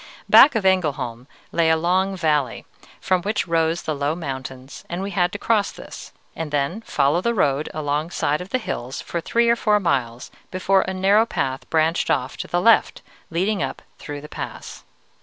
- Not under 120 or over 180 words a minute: No, average, 195 wpm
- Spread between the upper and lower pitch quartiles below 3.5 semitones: No, average, 5.0 semitones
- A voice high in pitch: No, medium, 165 Hz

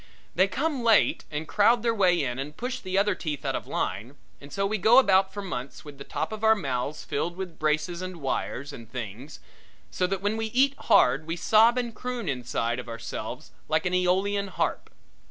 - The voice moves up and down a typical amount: No, wide, 7.0 semitones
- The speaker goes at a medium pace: No, fast, 210 wpm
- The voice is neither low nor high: Yes, medium, 180 Hz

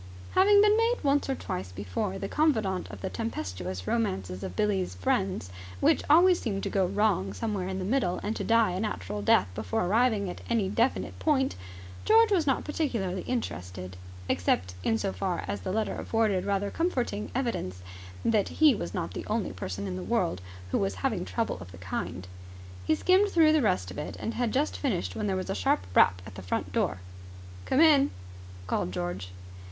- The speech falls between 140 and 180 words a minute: No, average, 195 wpm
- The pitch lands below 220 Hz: Yes, high, 190 Hz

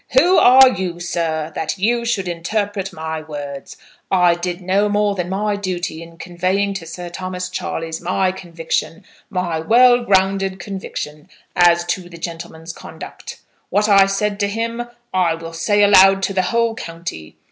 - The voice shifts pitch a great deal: No, average, 3.2 semitones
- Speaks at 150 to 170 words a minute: Yes, average, 160 wpm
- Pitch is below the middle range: No, medium, 185 Hz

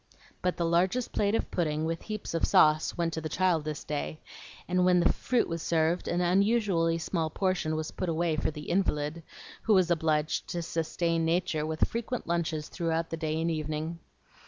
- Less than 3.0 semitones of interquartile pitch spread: Yes, narrow, 2.4 semitones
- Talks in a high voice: No, medium, 165 Hz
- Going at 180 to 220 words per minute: Yes, average, 190 wpm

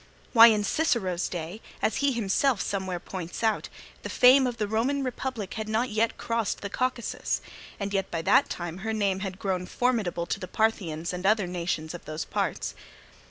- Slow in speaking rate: No, average, 185 wpm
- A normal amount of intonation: Yes, average, 4.2 semitones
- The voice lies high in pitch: Yes, high, 205 Hz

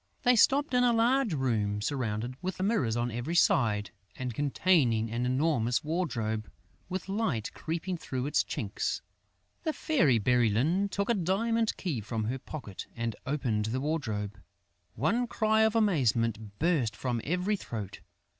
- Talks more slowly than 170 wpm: Yes, average, 145 wpm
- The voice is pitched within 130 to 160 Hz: Yes, low, 135 Hz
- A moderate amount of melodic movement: No, wide, 8.8 semitones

